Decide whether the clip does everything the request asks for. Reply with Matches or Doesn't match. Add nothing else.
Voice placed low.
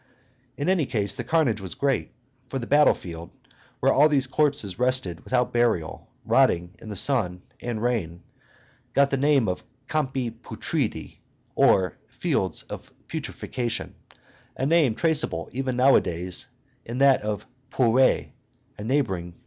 Matches